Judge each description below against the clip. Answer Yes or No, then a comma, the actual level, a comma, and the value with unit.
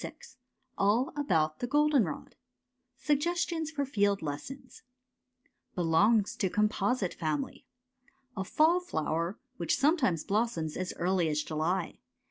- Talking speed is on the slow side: Yes, slow, 115 wpm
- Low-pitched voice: No, high, 200 Hz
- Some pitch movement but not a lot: No, wide, 8.9 semitones